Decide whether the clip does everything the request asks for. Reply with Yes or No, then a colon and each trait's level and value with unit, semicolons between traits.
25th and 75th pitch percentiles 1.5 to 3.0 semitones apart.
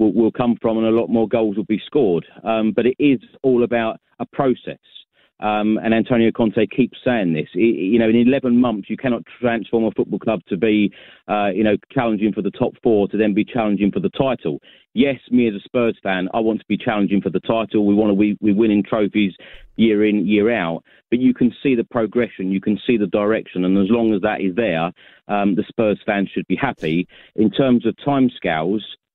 Yes: narrow, 2.4 semitones